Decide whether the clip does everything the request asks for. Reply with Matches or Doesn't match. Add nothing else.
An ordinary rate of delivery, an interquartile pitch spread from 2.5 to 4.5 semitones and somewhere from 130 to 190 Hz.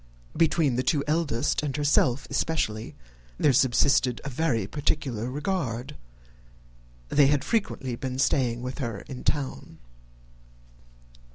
Doesn't match